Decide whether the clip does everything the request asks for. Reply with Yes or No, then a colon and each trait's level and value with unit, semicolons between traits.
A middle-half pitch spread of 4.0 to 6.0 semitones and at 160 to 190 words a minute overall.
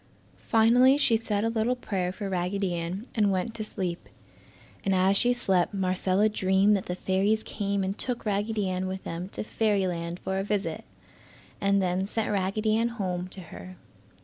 No: average, 2.7 semitones; average, 175 wpm